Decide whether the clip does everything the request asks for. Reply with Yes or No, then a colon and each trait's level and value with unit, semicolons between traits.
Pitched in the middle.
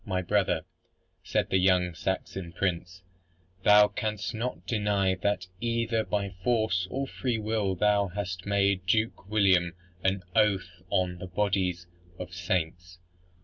No: very low, 95 Hz